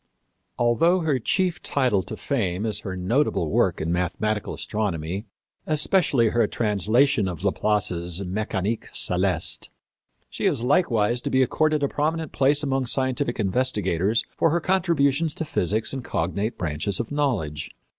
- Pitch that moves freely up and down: Yes, wide, 6.8 semitones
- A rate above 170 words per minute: No, average, 140 wpm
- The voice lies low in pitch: Yes, low, 115 Hz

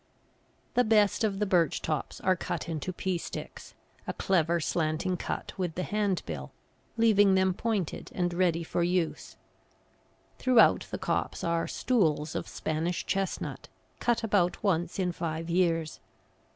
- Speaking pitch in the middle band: Yes, medium, 180 Hz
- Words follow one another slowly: No, average, 145 wpm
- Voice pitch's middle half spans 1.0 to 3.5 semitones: Yes, average, 3.0 semitones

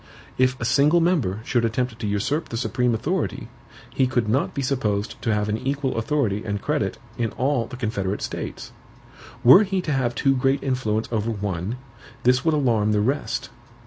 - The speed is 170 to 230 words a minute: Yes, average, 180 wpm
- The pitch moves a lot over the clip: No, average, 4.1 semitones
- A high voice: No, low, 125 Hz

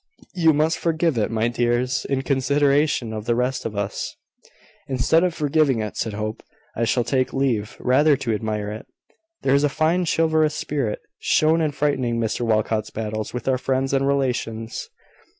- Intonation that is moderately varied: Yes, average, 4.6 semitones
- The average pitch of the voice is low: Yes, low, 130 Hz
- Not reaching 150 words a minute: No, average, 170 wpm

